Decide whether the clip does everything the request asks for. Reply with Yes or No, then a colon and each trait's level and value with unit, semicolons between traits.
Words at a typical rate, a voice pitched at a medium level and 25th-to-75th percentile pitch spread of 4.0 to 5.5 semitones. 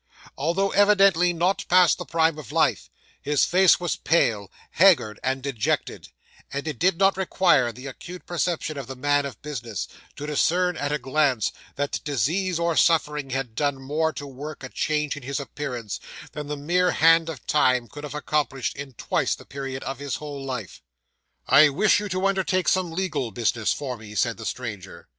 Yes: average, 185 wpm; medium, 145 Hz; average, 4.3 semitones